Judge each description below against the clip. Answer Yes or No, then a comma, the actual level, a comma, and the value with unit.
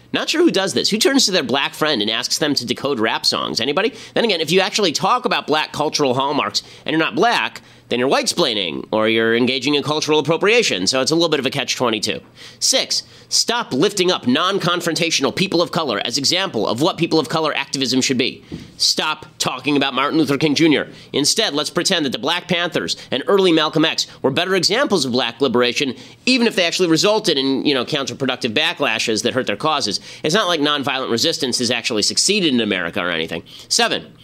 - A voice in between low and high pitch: Yes, medium, 150 Hz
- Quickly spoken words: Yes, fast, 210 wpm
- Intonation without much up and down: No, average, 5.2 semitones